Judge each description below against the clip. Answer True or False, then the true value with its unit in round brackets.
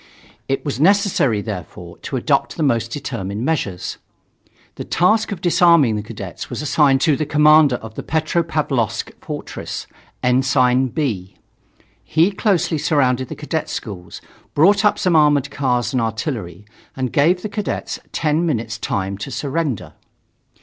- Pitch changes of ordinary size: False (5.8 semitones)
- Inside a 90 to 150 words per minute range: True (140 wpm)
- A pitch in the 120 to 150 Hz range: True (140 Hz)